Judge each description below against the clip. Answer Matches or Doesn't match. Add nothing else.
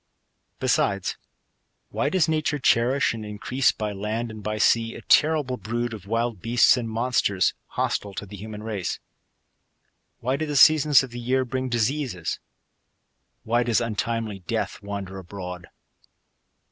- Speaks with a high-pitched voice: Doesn't match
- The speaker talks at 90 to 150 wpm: Matches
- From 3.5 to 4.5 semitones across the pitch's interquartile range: Matches